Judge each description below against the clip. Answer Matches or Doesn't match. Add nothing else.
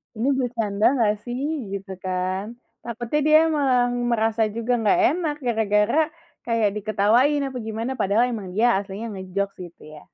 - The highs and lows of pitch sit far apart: Doesn't match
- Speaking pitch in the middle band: Doesn't match